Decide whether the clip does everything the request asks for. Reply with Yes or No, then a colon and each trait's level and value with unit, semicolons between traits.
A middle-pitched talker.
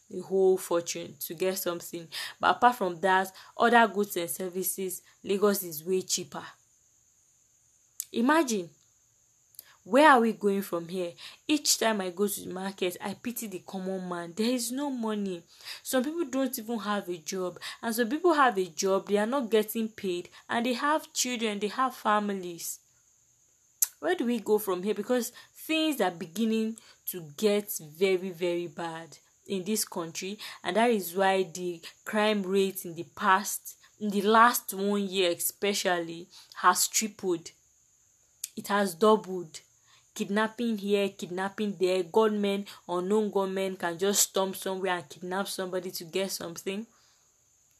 No: high, 195 Hz